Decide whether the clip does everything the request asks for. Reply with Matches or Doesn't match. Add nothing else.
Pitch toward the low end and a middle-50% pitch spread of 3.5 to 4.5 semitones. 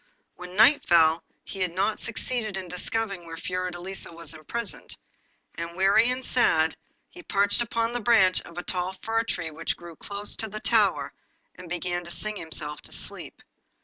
Doesn't match